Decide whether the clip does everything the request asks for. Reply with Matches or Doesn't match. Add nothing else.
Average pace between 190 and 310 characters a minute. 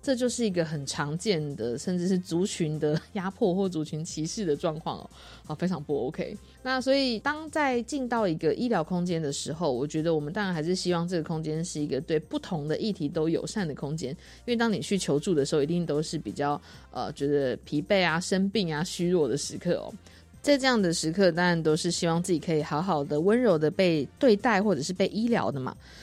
Doesn't match